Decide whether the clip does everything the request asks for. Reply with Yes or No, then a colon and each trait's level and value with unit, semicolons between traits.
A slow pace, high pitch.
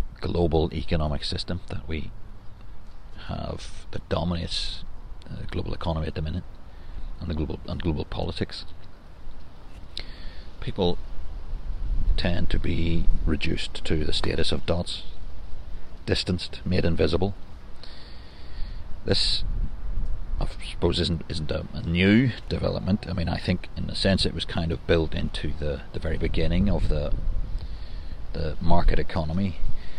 No: slow, 130 wpm; very low, 85 Hz